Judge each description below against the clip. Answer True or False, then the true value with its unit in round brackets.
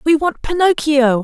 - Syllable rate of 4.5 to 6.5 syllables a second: False (4.2 syllables/s)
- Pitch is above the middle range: True (300 Hz)